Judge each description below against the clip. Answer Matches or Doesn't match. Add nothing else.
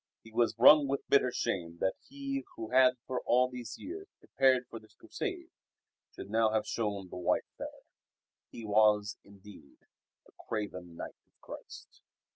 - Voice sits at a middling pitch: Doesn't match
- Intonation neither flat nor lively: Matches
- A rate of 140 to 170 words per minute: Matches